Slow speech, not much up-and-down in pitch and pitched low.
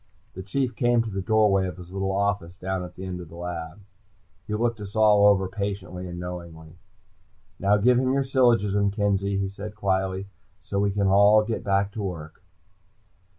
No: average, 190 wpm; narrow, 2.3 semitones; low, 100 Hz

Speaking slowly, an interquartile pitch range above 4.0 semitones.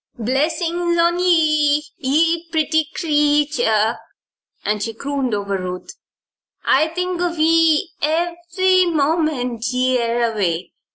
Yes: slow, 105 wpm; wide, 5.4 semitones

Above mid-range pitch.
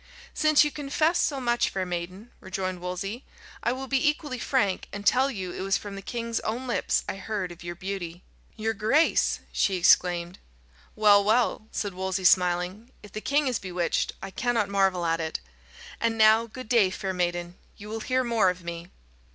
Yes: high, 200 Hz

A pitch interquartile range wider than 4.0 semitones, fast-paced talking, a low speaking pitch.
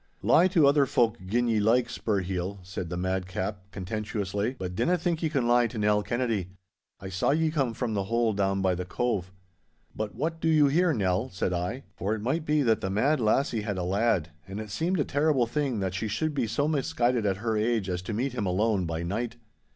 Yes: wide, 5.5 semitones; fast, 220 wpm; low, 110 Hz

